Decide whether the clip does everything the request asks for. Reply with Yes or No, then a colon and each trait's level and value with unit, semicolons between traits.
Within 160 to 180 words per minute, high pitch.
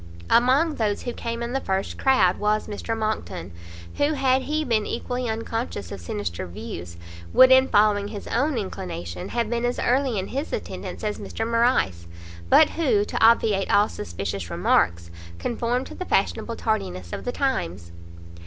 Yes: average, 165 wpm; high, 220 Hz